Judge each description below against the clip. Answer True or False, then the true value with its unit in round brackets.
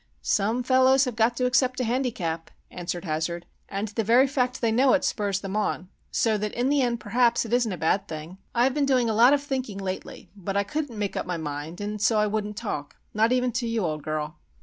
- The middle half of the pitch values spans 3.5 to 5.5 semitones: True (4.6 semitones)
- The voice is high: True (220 Hz)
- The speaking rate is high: True (235 wpm)